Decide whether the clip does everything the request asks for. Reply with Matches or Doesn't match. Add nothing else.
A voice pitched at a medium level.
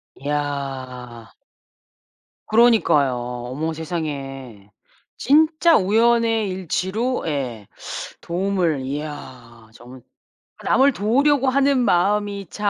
Matches